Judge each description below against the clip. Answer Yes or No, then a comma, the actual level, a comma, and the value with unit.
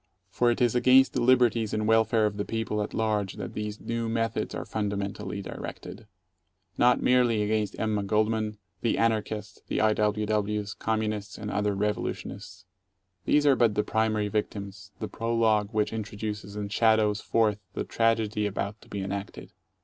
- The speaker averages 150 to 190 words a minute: Yes, average, 165 wpm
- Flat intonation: Yes, narrow, 1.4 semitones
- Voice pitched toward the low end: Yes, low, 110 Hz